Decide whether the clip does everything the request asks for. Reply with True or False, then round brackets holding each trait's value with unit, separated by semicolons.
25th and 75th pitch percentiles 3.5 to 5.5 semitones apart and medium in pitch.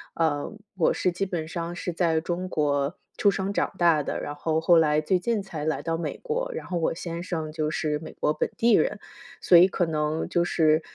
False (2.6 semitones; 165 Hz)